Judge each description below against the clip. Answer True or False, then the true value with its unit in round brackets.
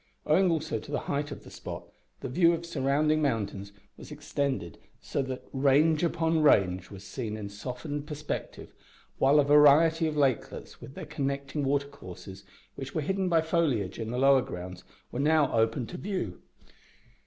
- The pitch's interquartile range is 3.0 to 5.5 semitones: True (4.5 semitones)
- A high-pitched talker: False (140 Hz)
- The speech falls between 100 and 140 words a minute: False (170 wpm)